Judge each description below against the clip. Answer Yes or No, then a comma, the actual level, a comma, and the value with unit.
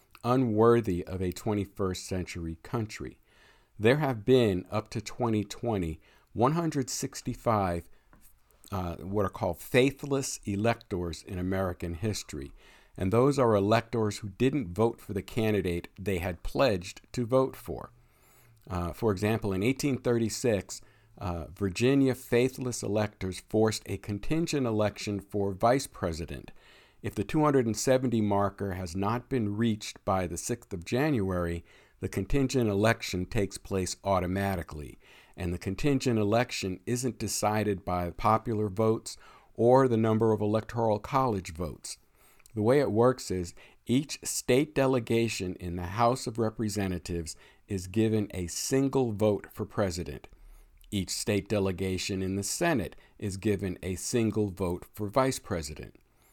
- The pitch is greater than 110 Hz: No, low, 105 Hz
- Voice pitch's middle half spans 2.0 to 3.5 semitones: No, average, 4.3 semitones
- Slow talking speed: Yes, slow, 130 wpm